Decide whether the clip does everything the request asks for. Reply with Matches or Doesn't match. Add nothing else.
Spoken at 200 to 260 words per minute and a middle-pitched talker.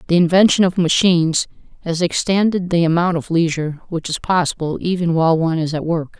Doesn't match